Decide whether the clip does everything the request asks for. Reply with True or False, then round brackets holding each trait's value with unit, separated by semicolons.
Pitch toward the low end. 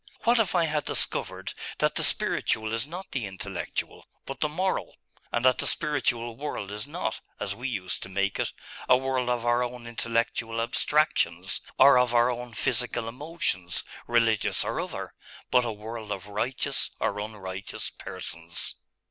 True (120 Hz)